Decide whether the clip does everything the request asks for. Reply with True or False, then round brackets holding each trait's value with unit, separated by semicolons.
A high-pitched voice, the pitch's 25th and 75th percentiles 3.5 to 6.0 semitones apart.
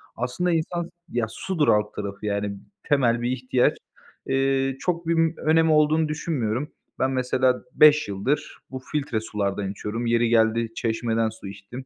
False (125 Hz; 5.3 semitones)